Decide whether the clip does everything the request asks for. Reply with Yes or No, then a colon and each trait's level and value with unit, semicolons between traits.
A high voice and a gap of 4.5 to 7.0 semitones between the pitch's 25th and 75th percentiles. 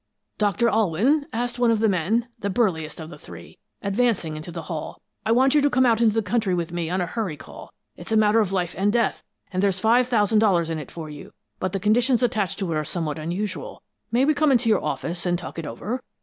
Yes: high, 205 Hz; average, 5.3 semitones